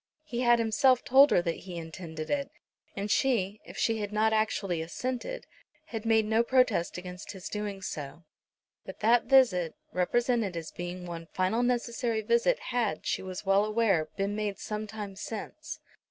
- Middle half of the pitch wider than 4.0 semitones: Yes, average, 4.5 semitones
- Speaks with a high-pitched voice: Yes, high, 210 Hz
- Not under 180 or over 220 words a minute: No, average, 170 wpm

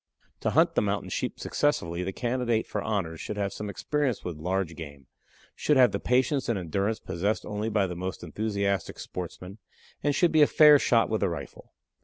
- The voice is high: No, low, 105 Hz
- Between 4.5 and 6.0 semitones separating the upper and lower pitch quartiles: Yes, average, 5.3 semitones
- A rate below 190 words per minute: No, average, 195 wpm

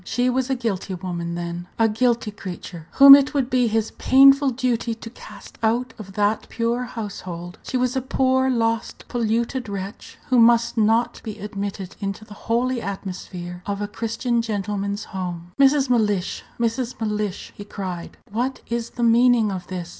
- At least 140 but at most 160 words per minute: No, average, 170 wpm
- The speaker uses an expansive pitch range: No, average, 3.8 semitones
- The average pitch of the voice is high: Yes, high, 225 Hz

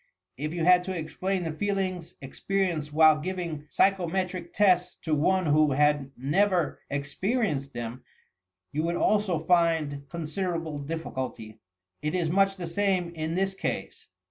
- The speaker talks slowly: No, average, 145 wpm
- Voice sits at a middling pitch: Yes, medium, 165 Hz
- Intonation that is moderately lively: Yes, average, 3.7 semitones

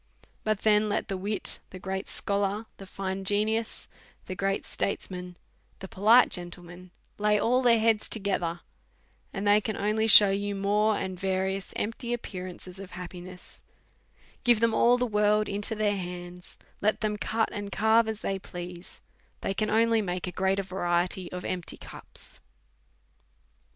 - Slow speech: No, average, 155 wpm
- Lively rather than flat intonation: No, narrow, 2.6 semitones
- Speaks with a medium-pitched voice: No, high, 200 Hz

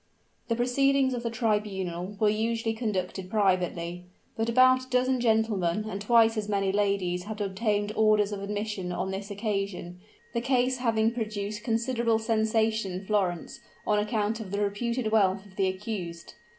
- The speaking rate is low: No, average, 160 wpm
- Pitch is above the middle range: Yes, high, 210 Hz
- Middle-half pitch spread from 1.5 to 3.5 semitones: Yes, narrow, 2.6 semitones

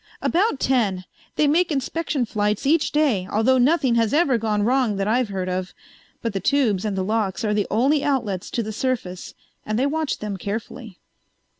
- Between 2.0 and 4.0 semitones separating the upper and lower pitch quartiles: No, average, 5.0 semitones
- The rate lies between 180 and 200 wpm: Yes, average, 185 wpm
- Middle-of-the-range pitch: No, high, 230 Hz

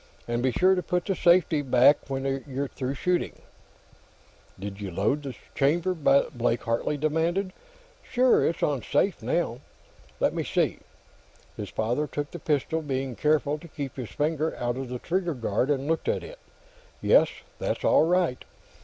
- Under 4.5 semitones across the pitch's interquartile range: No, average, 4.8 semitones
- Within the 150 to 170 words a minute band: Yes, average, 165 wpm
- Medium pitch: Yes, medium, 145 Hz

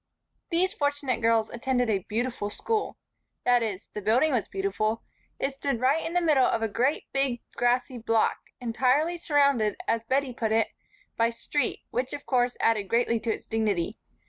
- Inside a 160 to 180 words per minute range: Yes, average, 170 wpm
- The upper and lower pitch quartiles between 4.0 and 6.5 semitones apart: No, average, 3.6 semitones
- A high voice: Yes, high, 245 Hz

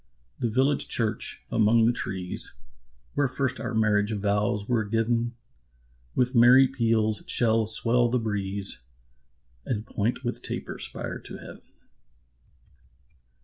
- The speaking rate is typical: No, slow, 120 wpm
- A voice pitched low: Yes, low, 115 Hz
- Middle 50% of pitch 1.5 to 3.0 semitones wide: Yes, narrow, 2.6 semitones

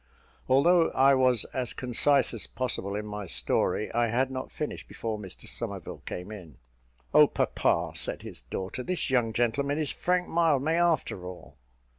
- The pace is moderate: Yes, average, 160 wpm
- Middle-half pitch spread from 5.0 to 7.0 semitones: Yes, average, 5.3 semitones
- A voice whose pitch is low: Yes, low, 125 Hz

